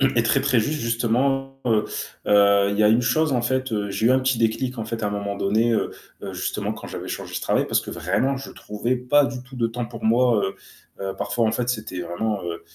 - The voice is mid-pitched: No, low, 115 Hz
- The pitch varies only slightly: No, average, 3.3 semitones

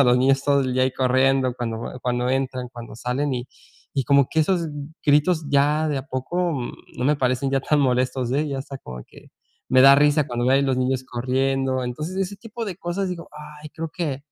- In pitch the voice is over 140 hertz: No, low, 135 Hz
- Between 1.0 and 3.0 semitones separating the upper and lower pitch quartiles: Yes, average, 2.7 semitones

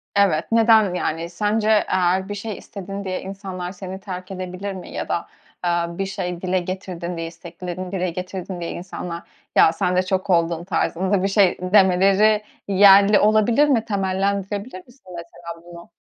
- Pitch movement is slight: Yes, narrow, 2.1 semitones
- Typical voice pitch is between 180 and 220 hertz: Yes, medium, 185 Hz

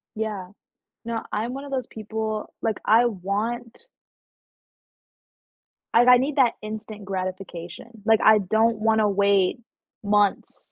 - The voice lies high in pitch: Yes, high, 220 Hz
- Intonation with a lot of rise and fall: No, narrow, 2.4 semitones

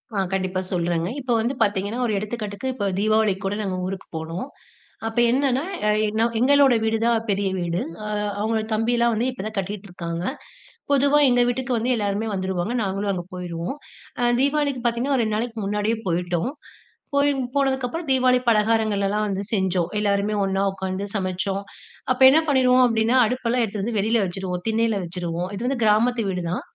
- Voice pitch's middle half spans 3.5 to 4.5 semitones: Yes, average, 4.1 semitones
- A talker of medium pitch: No, high, 215 Hz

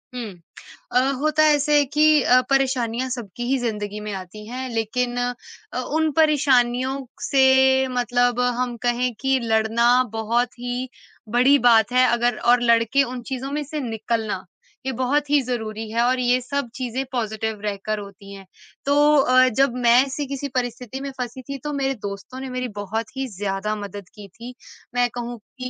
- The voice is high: Yes, high, 245 Hz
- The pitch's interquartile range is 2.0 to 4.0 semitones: Yes, average, 3.0 semitones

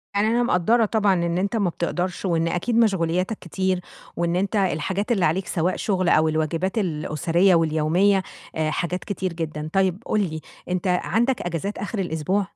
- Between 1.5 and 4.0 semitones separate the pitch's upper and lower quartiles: Yes, average, 3.1 semitones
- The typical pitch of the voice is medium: Yes, medium, 180 Hz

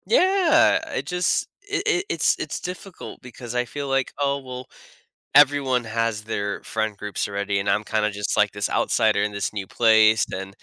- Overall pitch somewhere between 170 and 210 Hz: No, low, 115 Hz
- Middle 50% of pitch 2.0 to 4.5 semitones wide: No, wide, 5.6 semitones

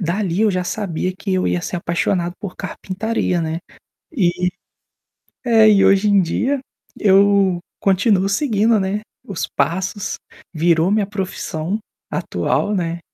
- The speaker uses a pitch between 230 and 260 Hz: No, high, 190 Hz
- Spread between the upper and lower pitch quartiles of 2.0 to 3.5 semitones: Yes, average, 2.8 semitones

